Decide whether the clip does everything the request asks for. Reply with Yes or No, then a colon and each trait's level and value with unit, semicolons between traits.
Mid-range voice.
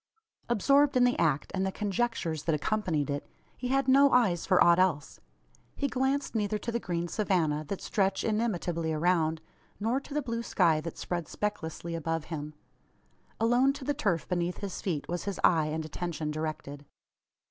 Yes: medium, 180 Hz